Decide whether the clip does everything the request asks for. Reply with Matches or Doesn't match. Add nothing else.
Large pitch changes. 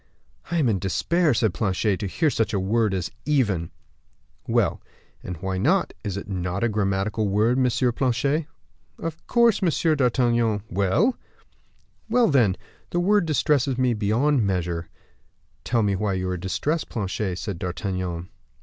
Matches